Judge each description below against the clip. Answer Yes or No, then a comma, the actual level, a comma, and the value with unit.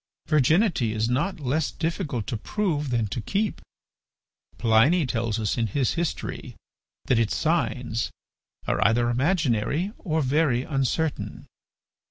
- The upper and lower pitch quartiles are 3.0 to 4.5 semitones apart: No, wide, 5.6 semitones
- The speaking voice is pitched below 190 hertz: Yes, low, 135 Hz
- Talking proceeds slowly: Yes, slow, 125 wpm